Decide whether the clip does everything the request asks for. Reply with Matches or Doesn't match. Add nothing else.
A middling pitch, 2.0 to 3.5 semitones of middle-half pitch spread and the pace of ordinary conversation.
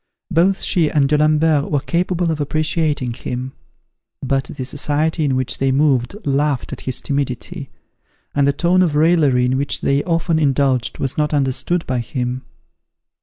Matches